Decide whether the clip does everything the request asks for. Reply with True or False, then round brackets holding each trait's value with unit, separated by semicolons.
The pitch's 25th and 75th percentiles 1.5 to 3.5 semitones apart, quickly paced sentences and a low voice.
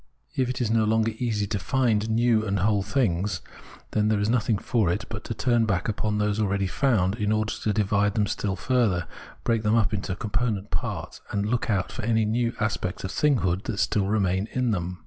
True (2.4 semitones; 220 wpm; 105 Hz)